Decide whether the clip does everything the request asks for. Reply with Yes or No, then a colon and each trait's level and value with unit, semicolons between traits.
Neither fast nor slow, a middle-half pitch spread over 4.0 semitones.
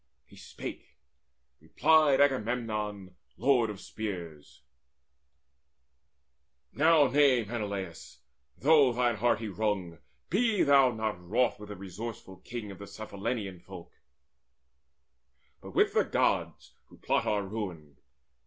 No: slow, 110 wpm; average, 4.8 semitones